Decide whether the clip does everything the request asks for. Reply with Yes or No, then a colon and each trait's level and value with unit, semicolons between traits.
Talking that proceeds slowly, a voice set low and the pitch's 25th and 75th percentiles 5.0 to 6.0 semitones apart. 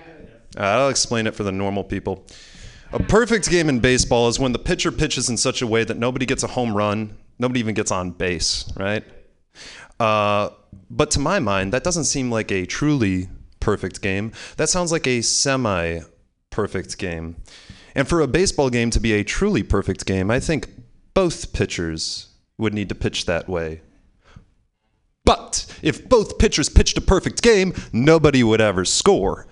No: average, 175 wpm; low, 110 Hz; average, 5.3 semitones